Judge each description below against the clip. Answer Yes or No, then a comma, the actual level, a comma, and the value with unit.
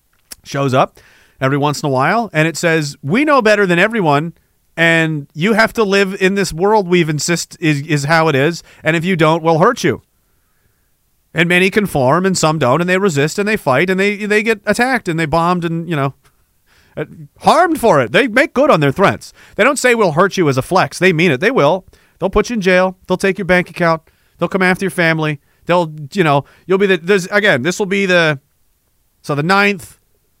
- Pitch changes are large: No, average, 4.5 semitones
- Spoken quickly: Yes, fast, 225 wpm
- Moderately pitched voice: Yes, medium, 175 Hz